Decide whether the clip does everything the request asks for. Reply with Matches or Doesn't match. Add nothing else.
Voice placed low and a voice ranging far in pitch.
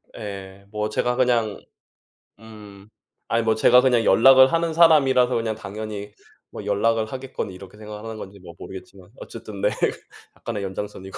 Doesn't match